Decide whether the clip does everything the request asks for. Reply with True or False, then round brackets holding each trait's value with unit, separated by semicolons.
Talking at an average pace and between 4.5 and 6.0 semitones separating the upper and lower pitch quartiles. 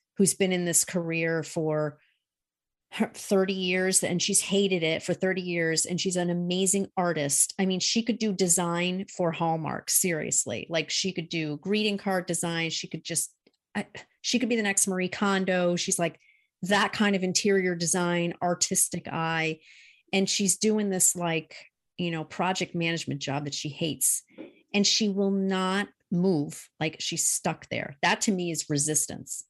False (170 wpm; 2.9 semitones)